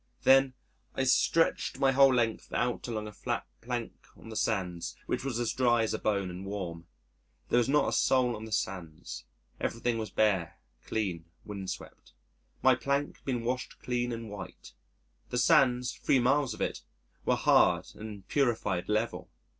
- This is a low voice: Yes, low, 115 Hz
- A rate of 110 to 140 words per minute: No, average, 170 wpm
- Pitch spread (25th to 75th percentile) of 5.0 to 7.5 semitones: No, average, 3.7 semitones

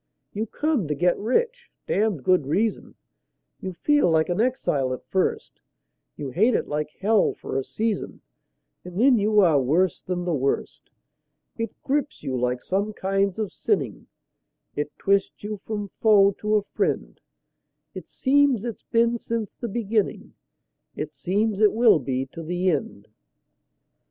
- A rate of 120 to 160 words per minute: Yes, average, 155 wpm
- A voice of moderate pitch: No, high, 200 Hz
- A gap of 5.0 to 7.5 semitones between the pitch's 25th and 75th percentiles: Yes, wide, 5.6 semitones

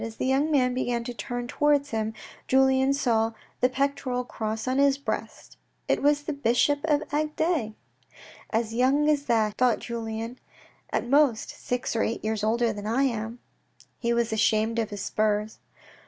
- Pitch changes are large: No, average, 3.8 semitones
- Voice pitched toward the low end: No, high, 245 Hz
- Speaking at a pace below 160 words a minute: No, average, 175 wpm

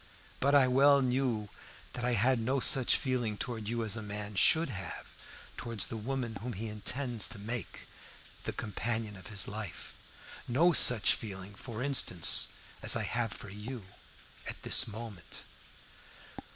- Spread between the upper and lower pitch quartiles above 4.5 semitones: No, average, 3.4 semitones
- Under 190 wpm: Yes, average, 155 wpm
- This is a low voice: Yes, low, 115 Hz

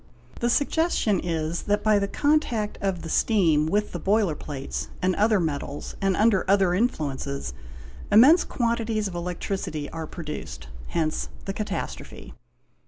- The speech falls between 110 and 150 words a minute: Yes, average, 140 wpm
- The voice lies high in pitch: Yes, high, 195 Hz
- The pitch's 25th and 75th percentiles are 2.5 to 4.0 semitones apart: No, average, 5.2 semitones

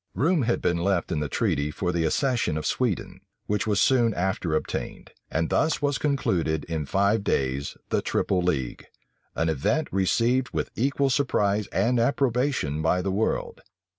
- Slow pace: No, average, 165 wpm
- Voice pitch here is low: Yes, low, 100 Hz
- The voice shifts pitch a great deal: Yes, wide, 7.5 semitones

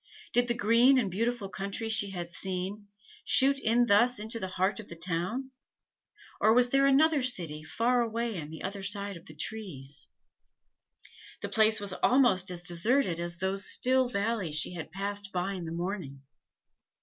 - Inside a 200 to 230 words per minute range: No, average, 175 wpm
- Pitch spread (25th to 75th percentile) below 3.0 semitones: No, average, 4.8 semitones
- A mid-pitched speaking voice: No, high, 200 Hz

